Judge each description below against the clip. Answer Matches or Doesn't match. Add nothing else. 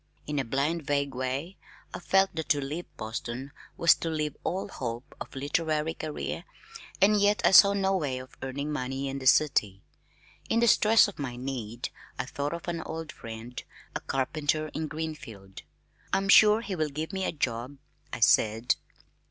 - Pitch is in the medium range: Matches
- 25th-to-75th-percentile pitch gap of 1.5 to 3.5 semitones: Doesn't match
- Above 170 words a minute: Matches